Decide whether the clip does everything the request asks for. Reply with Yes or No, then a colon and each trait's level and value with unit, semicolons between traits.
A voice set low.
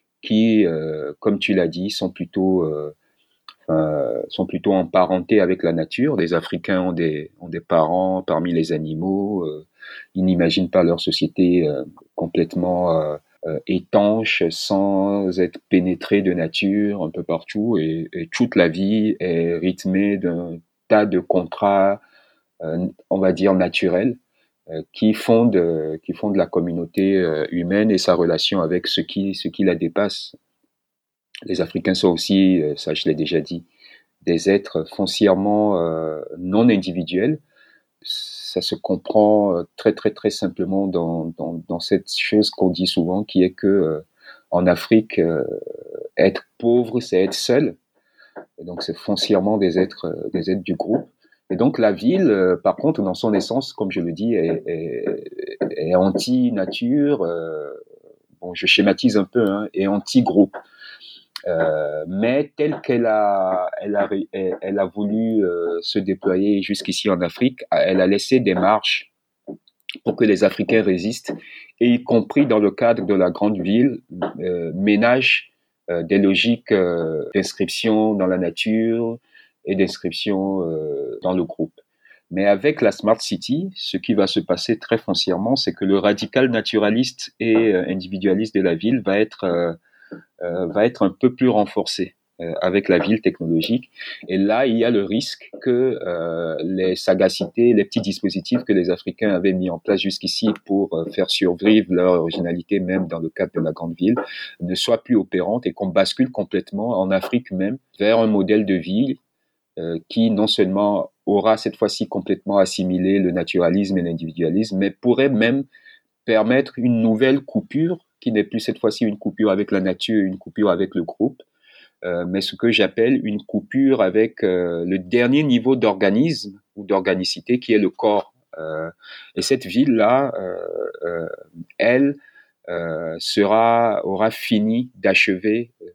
Yes: low, 100 Hz